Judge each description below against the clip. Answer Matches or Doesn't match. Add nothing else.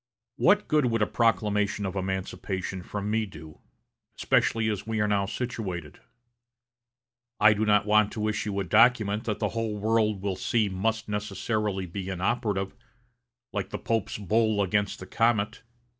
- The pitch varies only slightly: Matches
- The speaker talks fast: Doesn't match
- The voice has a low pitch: Matches